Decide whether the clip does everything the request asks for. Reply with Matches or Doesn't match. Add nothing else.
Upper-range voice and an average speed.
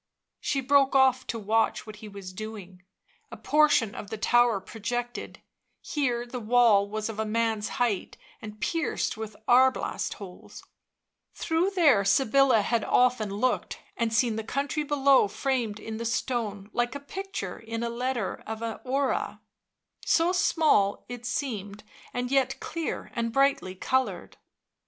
Matches